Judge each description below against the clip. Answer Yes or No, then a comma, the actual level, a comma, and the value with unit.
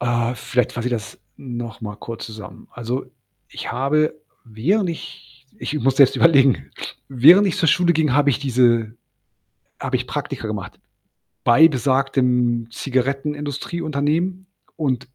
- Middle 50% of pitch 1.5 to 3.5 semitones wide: No, average, 3.9 semitones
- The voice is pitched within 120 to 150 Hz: Yes, low, 135 Hz